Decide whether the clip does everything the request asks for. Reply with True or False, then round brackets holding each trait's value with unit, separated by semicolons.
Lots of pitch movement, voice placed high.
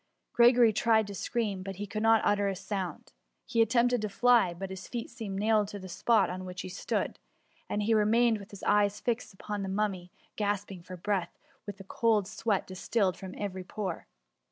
False (2.7 semitones; 205 Hz)